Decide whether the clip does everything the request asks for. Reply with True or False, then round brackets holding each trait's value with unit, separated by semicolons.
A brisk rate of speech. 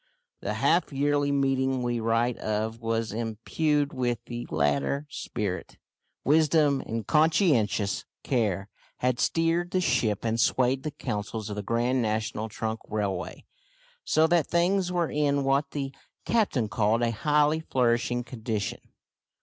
False (135 wpm)